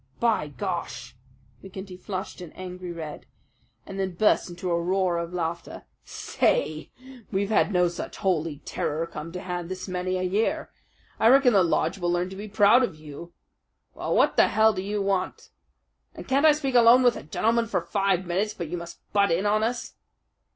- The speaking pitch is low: No, medium, 185 Hz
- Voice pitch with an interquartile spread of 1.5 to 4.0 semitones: Yes, average, 3.5 semitones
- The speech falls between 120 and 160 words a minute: No, average, 190 wpm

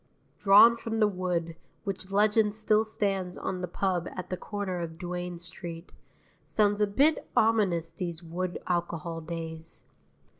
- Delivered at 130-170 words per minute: Yes, average, 145 wpm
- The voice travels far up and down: No, average, 3.3 semitones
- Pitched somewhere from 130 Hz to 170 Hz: No, medium, 185 Hz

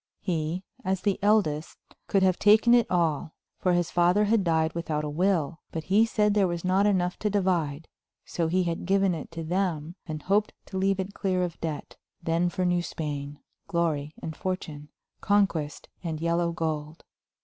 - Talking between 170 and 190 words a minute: Yes, average, 180 wpm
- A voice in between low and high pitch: Yes, medium, 175 Hz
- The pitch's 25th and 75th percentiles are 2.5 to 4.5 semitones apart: Yes, average, 3.2 semitones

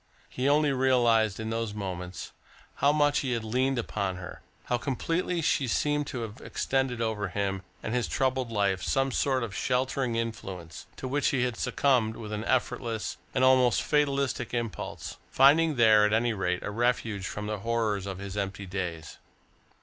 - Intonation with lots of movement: No, average, 4.2 semitones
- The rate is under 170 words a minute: No, average, 175 wpm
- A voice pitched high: No, low, 115 Hz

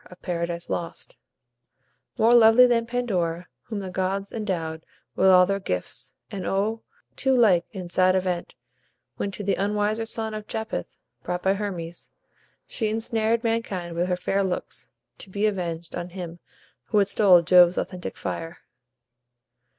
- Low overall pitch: No, high, 190 Hz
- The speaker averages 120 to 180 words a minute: Yes, average, 150 wpm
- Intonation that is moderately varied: Yes, average, 3.6 semitones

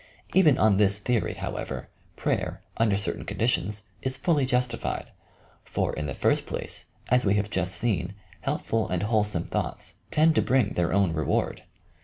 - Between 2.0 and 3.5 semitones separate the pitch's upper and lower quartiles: No, average, 4.7 semitones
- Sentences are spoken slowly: No, average, 165 wpm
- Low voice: Yes, low, 105 Hz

